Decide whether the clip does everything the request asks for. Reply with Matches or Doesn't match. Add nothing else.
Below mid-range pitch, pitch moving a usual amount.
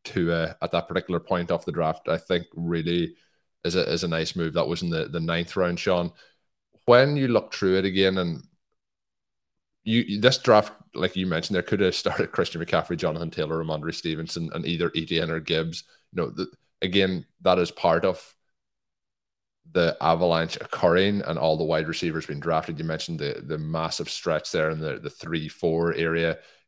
Doesn't match